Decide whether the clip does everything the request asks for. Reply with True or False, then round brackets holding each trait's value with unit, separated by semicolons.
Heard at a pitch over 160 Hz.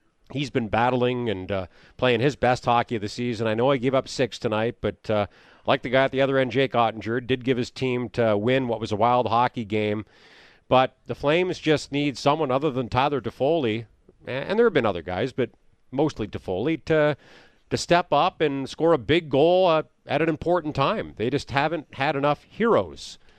False (130 Hz)